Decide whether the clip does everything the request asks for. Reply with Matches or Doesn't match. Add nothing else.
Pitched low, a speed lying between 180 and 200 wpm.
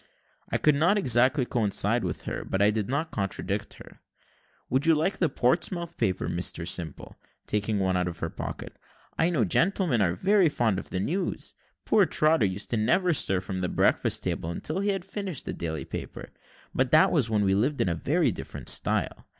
Matches